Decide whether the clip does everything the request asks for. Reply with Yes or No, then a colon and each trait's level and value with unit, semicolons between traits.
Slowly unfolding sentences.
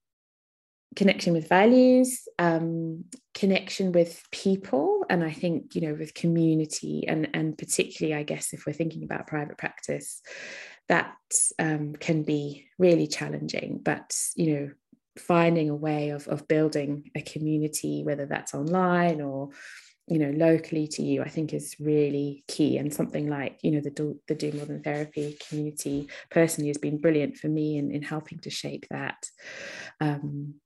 No: average, 160 wpm